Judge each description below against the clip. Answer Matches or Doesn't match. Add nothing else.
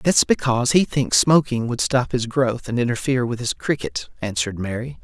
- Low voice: Matches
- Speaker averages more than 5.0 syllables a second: Matches